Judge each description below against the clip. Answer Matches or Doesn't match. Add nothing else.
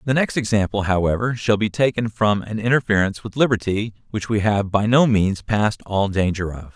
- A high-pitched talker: Doesn't match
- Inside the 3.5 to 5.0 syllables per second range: Doesn't match